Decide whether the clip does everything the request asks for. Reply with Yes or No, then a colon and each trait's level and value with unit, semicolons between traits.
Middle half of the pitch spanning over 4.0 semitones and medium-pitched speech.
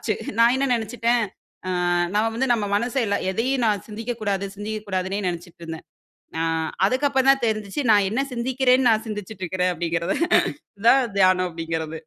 No: average, 4.6 semitones; high, 210 Hz